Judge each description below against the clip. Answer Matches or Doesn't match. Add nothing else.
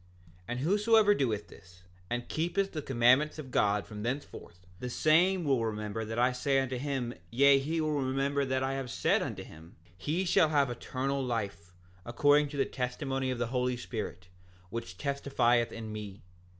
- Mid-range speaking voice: Doesn't match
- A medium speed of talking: Matches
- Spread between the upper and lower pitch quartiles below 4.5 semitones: Matches